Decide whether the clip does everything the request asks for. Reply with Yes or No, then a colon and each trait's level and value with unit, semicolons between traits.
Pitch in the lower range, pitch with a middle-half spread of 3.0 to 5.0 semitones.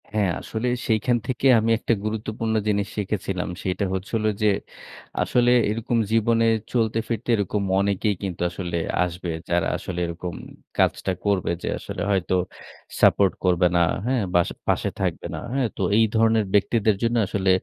Yes: low, 105 Hz; average, 3.3 semitones